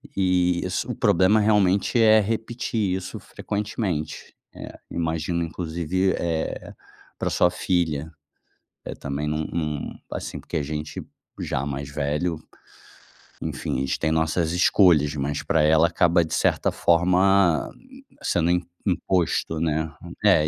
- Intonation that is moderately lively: Yes, average, 3.2 semitones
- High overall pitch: No, very low, 85 Hz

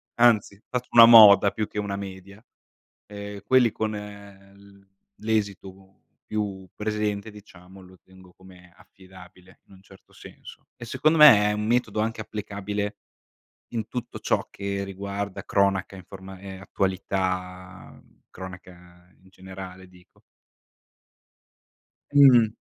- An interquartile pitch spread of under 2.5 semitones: Yes, narrow, 2.1 semitones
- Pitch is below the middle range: Yes, low, 100 Hz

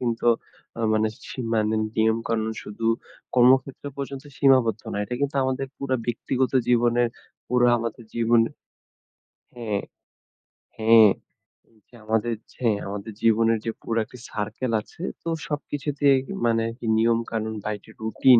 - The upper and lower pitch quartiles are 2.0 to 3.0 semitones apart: Yes, narrow, 2.5 semitones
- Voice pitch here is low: Yes, low, 115 Hz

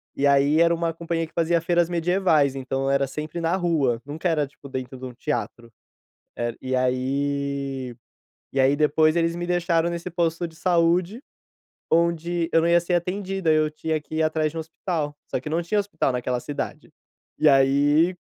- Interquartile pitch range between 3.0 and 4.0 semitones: Yes, average, 3.6 semitones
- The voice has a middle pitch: Yes, medium, 160 Hz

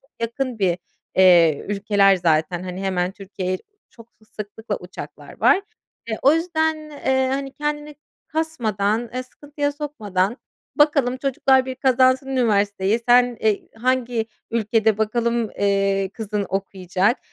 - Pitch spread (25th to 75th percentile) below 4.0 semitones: No, average, 5.0 semitones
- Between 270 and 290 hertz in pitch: No, high, 225 Hz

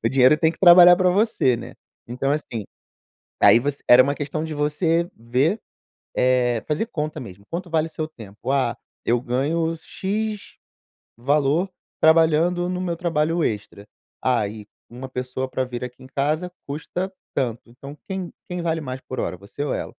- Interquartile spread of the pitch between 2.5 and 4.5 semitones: No, average, 5.0 semitones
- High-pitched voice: No, medium, 145 Hz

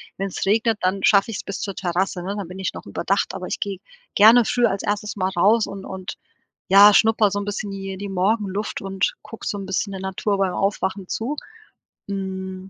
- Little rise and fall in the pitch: Yes, narrow, 1.6 semitones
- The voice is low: No, high, 195 Hz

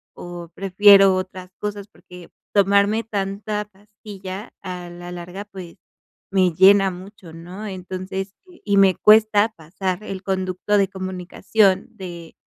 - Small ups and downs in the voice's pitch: Yes, narrow, 1.9 semitones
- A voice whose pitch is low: No, high, 190 Hz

